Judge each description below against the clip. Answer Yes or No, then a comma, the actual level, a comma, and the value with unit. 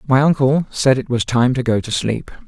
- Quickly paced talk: Yes, fast, 245 wpm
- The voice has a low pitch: Yes, low, 125 Hz